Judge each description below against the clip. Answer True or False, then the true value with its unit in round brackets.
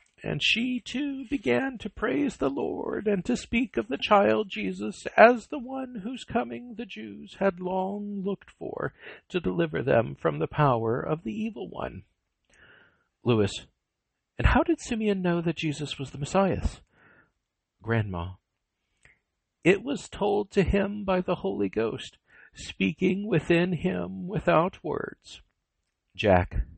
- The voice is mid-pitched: True (180 Hz)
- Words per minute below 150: True (140 wpm)